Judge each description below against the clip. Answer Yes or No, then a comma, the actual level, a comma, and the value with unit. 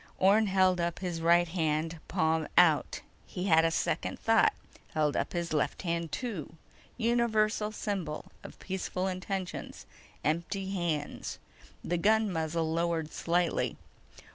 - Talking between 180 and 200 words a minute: No, slow, 135 wpm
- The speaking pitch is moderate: Yes, medium, 175 Hz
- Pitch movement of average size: Yes, average, 3.0 semitones